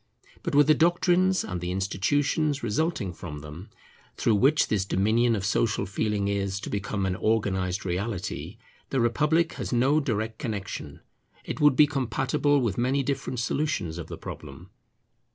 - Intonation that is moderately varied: No, wide, 6.7 semitones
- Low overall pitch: Yes, low, 110 Hz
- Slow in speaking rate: No, average, 155 wpm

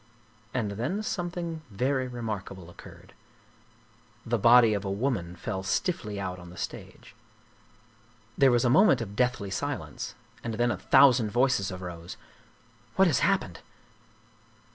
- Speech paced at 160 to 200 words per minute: No, average, 150 wpm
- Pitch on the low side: Yes, low, 115 Hz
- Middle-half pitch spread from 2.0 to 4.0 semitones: No, average, 5.2 semitones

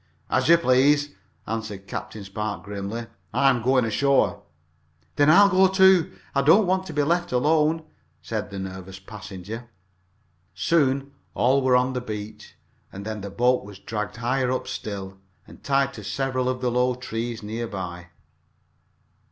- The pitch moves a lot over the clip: No, average, 4.8 semitones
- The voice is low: Yes, low, 125 Hz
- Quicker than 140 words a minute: Yes, average, 160 wpm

